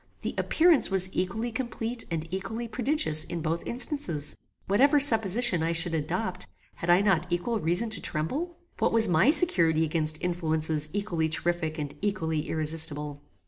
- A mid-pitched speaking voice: Yes, medium, 175 Hz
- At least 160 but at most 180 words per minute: No, average, 150 wpm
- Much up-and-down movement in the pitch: Yes, wide, 6.0 semitones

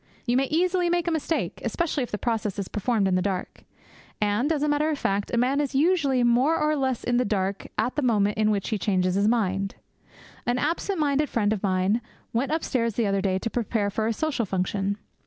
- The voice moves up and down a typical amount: No, wide, 6.3 semitones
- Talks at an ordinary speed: No, fast, 225 wpm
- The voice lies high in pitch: Yes, high, 235 Hz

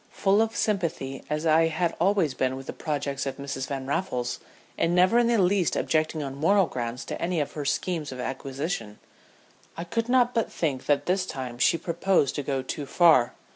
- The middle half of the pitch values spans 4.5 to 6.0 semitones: Yes, average, 5.2 semitones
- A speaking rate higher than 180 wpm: Yes, average, 200 wpm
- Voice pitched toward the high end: No, medium, 155 Hz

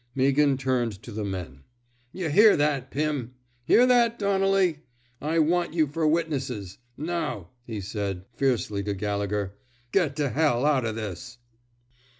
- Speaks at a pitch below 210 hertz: Yes, low, 135 Hz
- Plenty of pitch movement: Yes, wide, 7.3 semitones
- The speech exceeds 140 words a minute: Yes, average, 150 wpm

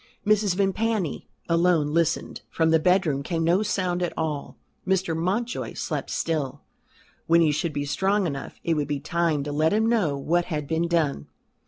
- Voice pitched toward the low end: No, medium, 165 Hz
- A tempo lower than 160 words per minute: No, average, 175 wpm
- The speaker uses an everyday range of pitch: Yes, average, 3.7 semitones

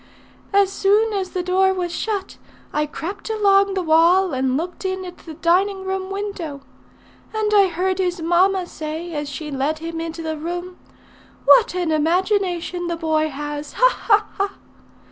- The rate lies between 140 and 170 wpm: Yes, average, 165 wpm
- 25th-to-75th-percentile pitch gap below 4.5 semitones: Yes, average, 3.4 semitones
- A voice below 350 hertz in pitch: No, very high, 360 Hz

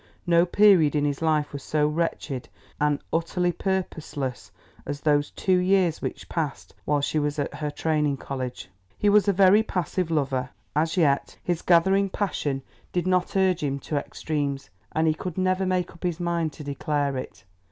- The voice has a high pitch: No, medium, 160 Hz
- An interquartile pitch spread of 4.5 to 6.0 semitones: No, average, 3.8 semitones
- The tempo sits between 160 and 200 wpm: Yes, average, 175 wpm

